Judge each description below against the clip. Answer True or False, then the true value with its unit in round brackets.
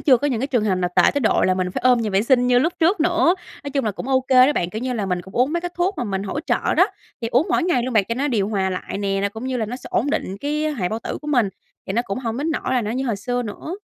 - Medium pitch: False (245 Hz)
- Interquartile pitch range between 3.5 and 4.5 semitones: False (5.5 semitones)